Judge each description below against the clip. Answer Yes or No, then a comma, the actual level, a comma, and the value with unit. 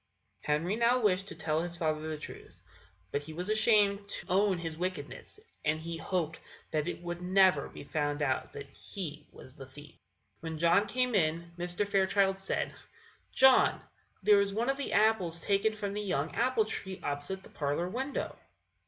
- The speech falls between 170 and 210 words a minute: Yes, average, 180 wpm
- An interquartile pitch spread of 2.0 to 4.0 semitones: No, average, 4.5 semitones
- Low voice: No, medium, 180 Hz